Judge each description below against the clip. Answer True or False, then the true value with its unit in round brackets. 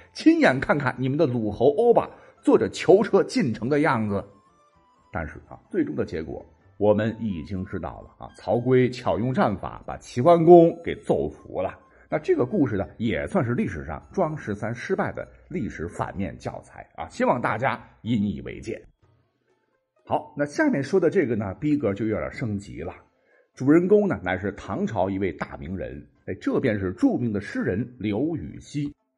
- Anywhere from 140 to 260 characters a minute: True (255 characters per minute)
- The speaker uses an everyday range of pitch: False (7.5 semitones)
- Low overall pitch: True (120 Hz)